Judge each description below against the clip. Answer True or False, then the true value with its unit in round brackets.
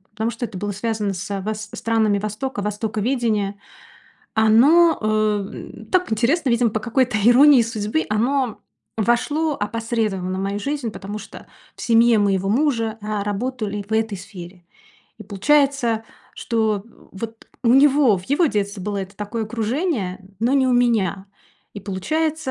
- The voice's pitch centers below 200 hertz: False (220 Hz)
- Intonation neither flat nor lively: True (3.4 semitones)